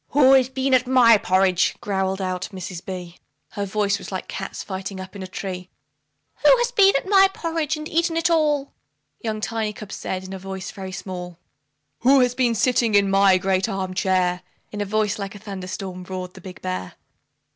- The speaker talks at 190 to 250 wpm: Yes, average, 200 wpm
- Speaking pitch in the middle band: No, high, 195 Hz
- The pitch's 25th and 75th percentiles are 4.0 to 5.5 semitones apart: Yes, average, 5.1 semitones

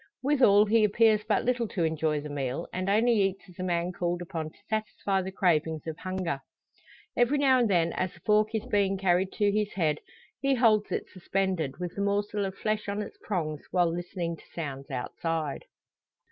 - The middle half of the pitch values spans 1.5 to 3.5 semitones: No, average, 4.1 semitones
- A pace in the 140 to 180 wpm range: No, average, 195 wpm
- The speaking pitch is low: No, high, 190 Hz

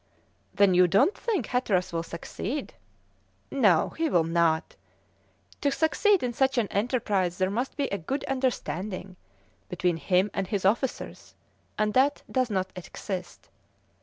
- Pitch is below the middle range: No, high, 200 Hz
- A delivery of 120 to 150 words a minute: Yes, average, 140 wpm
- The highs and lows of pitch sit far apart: Yes, wide, 6.2 semitones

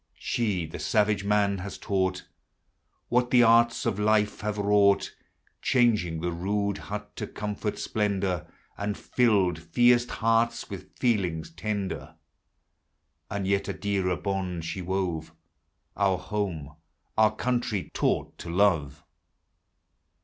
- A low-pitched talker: Yes, low, 100 Hz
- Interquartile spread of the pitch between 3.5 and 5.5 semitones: No, average, 2.8 semitones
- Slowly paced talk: Yes, slow, 125 wpm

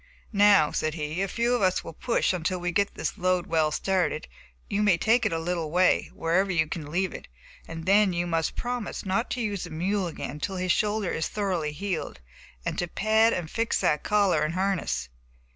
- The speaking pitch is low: No, medium, 185 Hz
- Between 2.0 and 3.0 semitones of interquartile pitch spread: No, average, 3.8 semitones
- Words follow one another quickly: Yes, fast, 210 wpm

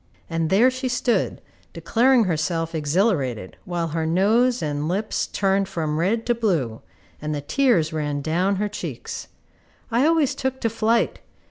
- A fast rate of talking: No, average, 150 wpm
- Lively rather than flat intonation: Yes, wide, 6.7 semitones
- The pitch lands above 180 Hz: Yes, high, 190 Hz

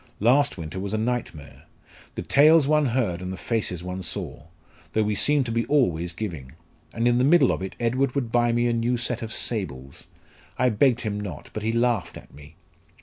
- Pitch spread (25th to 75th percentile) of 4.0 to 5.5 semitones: Yes, average, 5.2 semitones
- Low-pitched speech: Yes, low, 115 Hz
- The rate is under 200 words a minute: No, fast, 205 wpm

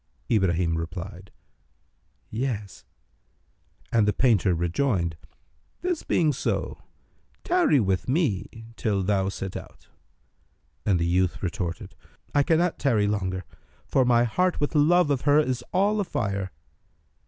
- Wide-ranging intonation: Yes, wide, 7.6 semitones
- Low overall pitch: Yes, low, 105 Hz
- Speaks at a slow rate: Yes, slow, 120 wpm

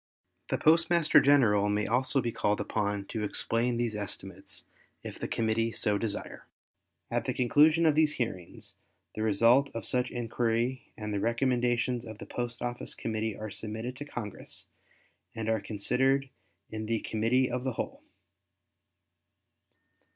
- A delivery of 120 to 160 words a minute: Yes, average, 145 wpm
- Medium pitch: No, low, 115 Hz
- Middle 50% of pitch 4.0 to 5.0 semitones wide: No, average, 2.9 semitones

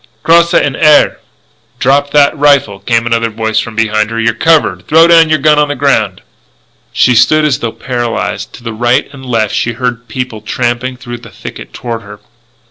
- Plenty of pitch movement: No, average, 4.0 semitones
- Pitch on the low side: Yes, low, 120 Hz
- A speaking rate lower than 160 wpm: No, average, 185 wpm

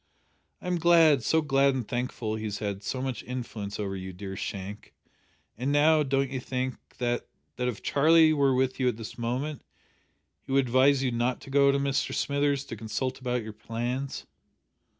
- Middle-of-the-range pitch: No, low, 130 Hz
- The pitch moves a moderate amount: Yes, average, 3.5 semitones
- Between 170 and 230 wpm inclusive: Yes, average, 190 wpm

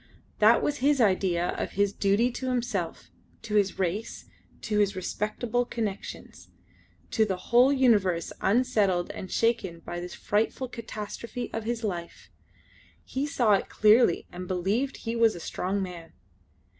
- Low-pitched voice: No, high, 210 Hz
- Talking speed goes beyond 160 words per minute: No, average, 145 wpm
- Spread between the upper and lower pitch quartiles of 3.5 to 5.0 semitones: Yes, average, 4.2 semitones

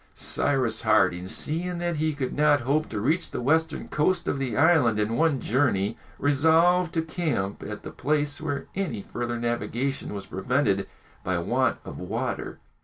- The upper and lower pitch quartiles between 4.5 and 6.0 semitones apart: Yes, wide, 5.6 semitones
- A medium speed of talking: Yes, average, 165 wpm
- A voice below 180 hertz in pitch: Yes, medium, 140 Hz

